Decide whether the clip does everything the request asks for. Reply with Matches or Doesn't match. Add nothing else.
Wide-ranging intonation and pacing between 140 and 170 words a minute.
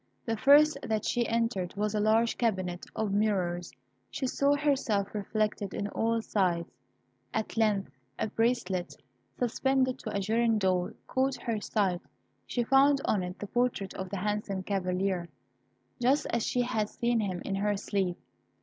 Doesn't match